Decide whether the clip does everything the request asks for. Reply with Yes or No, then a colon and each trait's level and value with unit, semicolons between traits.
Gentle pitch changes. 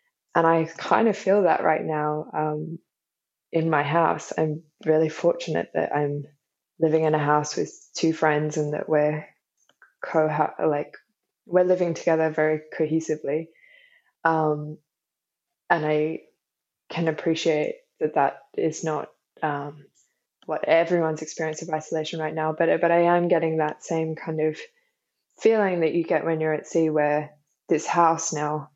Yes: narrow, 1.6 semitones